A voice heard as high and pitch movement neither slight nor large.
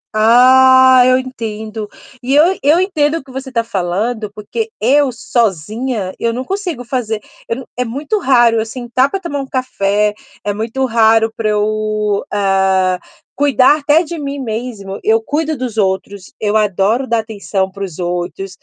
Yes: high, 230 Hz; average, 4.1 semitones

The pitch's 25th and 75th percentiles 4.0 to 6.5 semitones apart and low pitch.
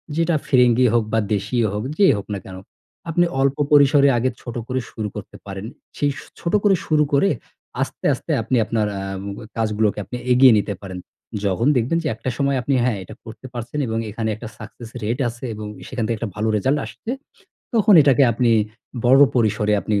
Yes: average, 4.4 semitones; low, 120 Hz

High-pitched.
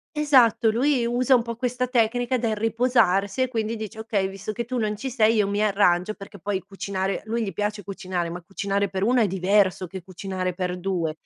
Yes: high, 210 Hz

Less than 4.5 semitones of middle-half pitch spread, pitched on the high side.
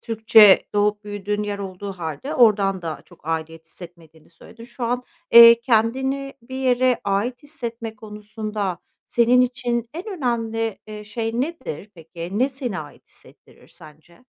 Yes: average, 4.0 semitones; high, 220 Hz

